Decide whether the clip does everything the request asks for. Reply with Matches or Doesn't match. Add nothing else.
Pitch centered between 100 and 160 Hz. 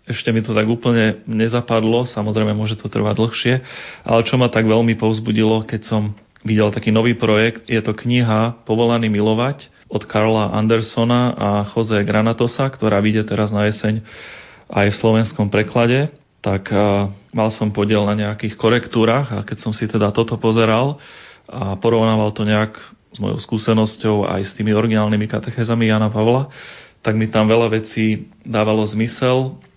Matches